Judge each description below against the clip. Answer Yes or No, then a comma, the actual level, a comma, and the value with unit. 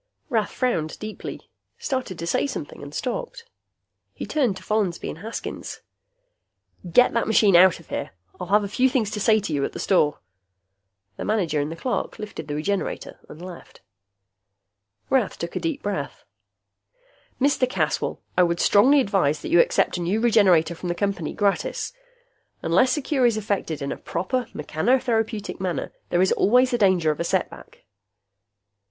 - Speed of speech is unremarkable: Yes, average, 170 wpm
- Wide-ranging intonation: Yes, wide, 5.9 semitones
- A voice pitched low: No, high, 205 Hz